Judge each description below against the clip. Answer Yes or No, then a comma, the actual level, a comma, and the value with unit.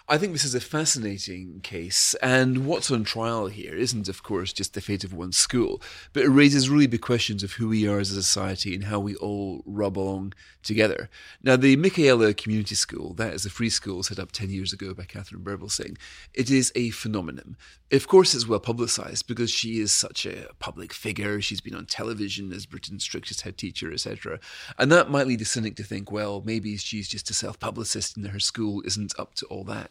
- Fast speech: Yes, fast, 215 wpm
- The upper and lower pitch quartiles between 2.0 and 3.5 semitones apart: Yes, average, 3.2 semitones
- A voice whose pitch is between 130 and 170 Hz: No, low, 105 Hz